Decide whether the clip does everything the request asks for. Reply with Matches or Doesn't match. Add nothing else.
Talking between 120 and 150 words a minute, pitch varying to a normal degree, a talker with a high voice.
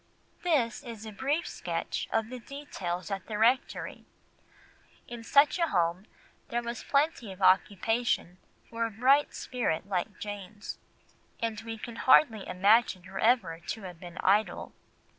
Matches